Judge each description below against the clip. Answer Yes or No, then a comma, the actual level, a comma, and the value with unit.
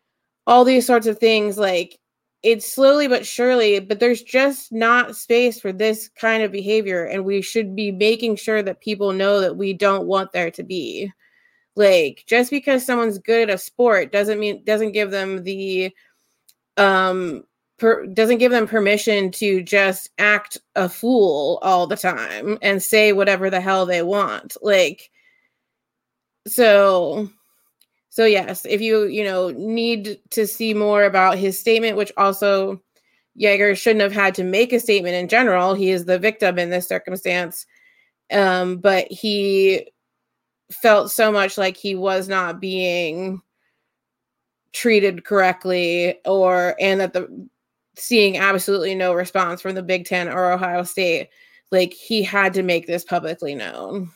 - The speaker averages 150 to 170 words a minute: Yes, average, 155 wpm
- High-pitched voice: Yes, high, 200 Hz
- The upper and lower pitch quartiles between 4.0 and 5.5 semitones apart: No, average, 2.9 semitones